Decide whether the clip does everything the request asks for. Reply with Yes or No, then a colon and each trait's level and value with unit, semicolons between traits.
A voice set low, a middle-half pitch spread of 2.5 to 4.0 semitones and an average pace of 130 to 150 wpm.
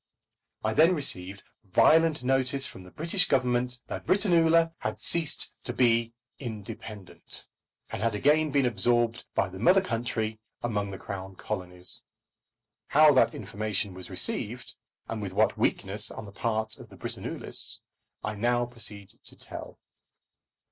No: low, 115 Hz; average, 5.2 semitones; average, 140 wpm